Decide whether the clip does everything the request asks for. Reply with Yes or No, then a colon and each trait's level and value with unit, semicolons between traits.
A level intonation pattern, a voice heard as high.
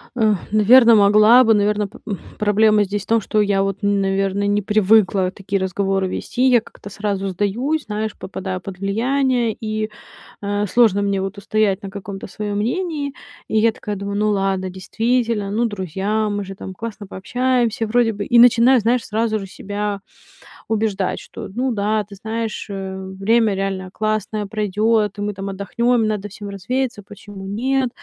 Yes: narrow, 2.3 semitones; high, 210 Hz